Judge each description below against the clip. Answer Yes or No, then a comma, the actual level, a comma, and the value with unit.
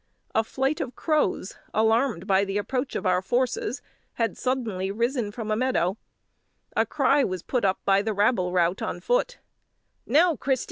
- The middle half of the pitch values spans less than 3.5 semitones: No, average, 5.2 semitones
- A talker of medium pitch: No, high, 225 Hz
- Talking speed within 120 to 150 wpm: No, average, 170 wpm